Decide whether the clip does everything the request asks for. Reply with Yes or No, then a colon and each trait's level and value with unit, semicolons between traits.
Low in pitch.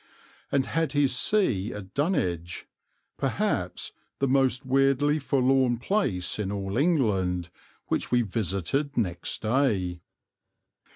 Yes: low, 125 Hz